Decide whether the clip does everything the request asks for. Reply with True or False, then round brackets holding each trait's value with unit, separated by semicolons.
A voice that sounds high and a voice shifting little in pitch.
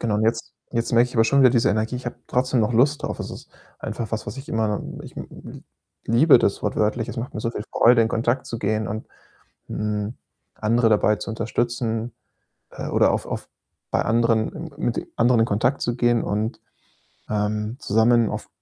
False (115 Hz; 1.9 semitones)